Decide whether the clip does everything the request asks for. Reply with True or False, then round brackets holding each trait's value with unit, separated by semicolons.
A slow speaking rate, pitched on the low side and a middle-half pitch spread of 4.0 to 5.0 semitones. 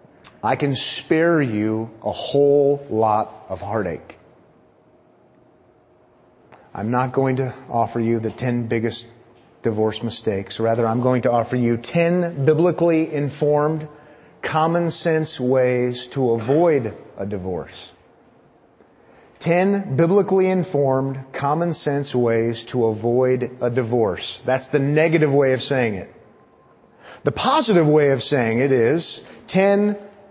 True (120 wpm; 130 Hz; 4.7 semitones)